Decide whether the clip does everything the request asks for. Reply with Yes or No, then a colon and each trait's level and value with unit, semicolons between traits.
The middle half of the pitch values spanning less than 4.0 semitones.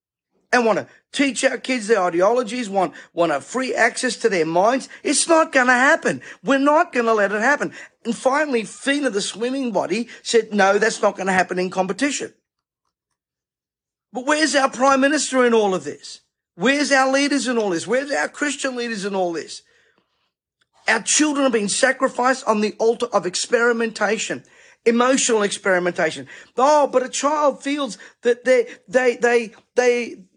No: average, 4.3 semitones